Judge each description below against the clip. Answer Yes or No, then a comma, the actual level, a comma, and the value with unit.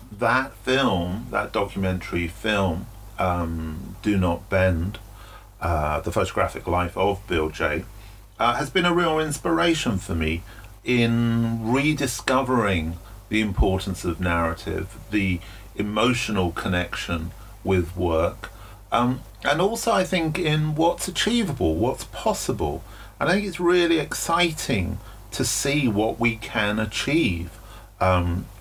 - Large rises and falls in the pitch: Yes, wide, 6.1 semitones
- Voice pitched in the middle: No, low, 105 Hz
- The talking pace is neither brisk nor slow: No, slow, 120 wpm